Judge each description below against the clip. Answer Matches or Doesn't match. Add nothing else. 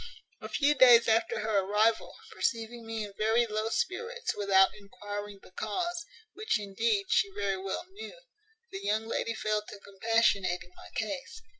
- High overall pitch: Matches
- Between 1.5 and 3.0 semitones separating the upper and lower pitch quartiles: Matches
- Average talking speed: Matches